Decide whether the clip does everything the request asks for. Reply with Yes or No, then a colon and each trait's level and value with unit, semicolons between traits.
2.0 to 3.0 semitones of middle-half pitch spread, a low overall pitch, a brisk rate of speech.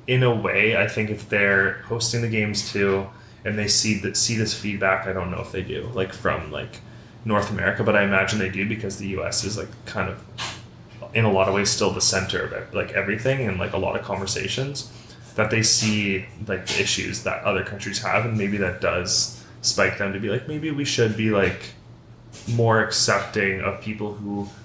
Yes: narrow, 2.6 semitones; low, 105 Hz; fast, 215 wpm